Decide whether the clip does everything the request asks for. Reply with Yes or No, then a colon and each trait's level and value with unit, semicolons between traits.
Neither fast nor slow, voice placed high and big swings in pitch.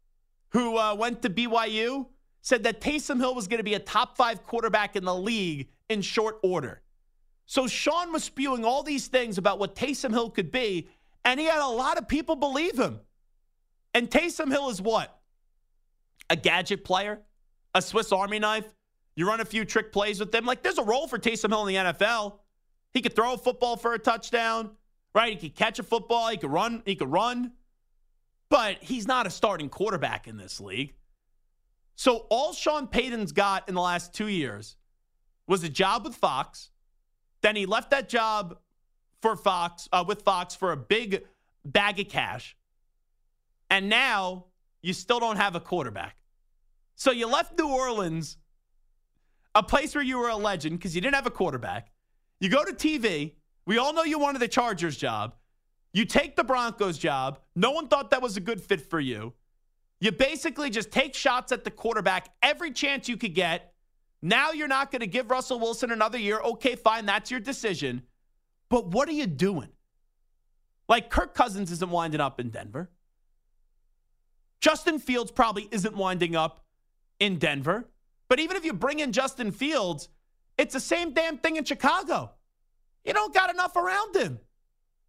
Yes: average, 180 wpm; high, 220 Hz; wide, 6.2 semitones